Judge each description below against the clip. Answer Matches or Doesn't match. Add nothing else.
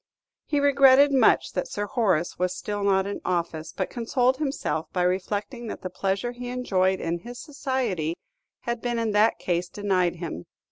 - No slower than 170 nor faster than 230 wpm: Matches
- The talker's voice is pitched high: Matches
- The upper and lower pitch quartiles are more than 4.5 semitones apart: Matches